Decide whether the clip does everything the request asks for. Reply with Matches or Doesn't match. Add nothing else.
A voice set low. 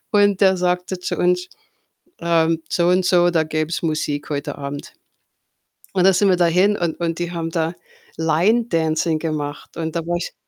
Doesn't match